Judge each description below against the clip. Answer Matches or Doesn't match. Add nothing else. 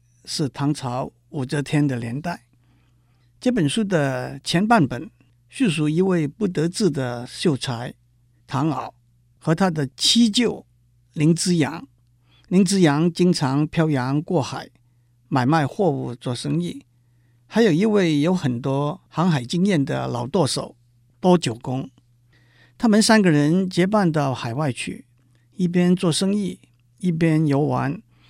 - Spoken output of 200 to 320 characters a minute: Doesn't match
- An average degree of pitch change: Doesn't match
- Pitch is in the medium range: Matches